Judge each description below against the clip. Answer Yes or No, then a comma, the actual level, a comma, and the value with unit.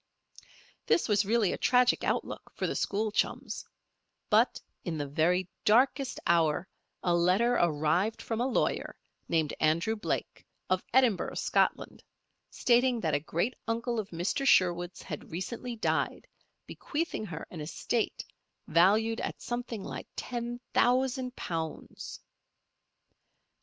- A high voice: Yes, high, 210 Hz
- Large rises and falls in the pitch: Yes, wide, 5.9 semitones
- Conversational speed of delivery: No, slow, 125 wpm